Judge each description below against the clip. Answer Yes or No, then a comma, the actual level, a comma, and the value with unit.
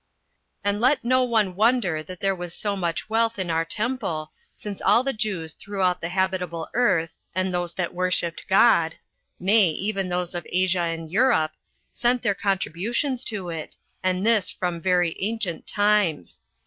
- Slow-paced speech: No, average, 165 wpm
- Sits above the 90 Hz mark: Yes, medium, 185 Hz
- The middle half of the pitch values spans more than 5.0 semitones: No, average, 3.7 semitones